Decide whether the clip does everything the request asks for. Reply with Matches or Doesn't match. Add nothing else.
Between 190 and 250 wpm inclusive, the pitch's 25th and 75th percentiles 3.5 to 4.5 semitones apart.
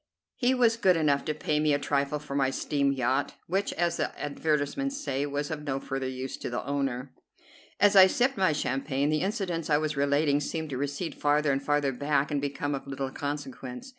Doesn't match